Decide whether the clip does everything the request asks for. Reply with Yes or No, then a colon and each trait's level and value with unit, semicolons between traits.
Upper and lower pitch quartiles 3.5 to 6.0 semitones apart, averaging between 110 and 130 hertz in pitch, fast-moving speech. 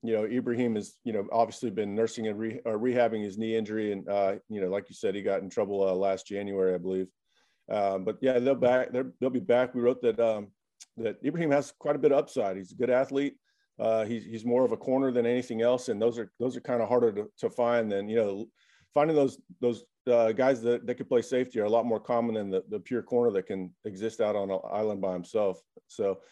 No: average, 3.1 semitones; low, 115 Hz; fast, 255 wpm